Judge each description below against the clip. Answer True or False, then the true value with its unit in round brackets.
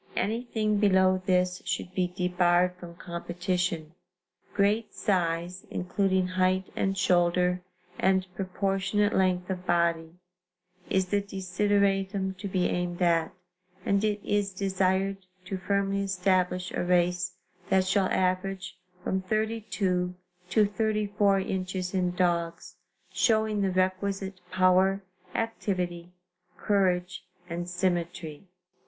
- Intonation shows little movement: True (1.7 semitones)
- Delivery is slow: True (110 wpm)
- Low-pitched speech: False (185 Hz)